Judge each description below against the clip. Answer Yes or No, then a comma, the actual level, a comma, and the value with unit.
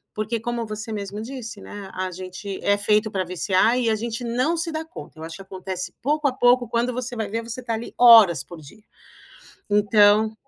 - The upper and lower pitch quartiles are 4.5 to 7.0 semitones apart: No, average, 3.5 semitones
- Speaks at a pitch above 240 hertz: No, high, 220 Hz